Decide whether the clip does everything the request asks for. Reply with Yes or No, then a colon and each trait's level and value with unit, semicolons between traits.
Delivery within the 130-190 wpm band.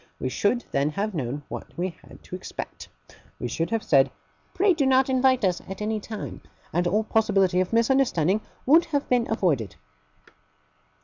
Yes: average, 170 wpm